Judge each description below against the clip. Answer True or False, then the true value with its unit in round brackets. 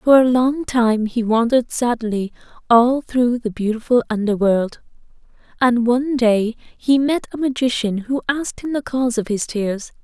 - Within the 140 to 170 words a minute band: True (160 wpm)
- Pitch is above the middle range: True (240 Hz)